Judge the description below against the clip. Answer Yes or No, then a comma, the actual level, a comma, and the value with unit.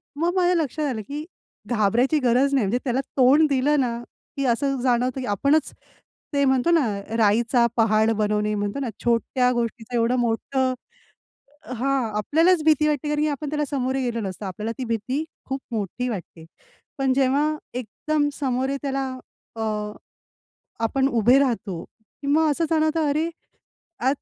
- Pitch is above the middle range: Yes, very high, 260 Hz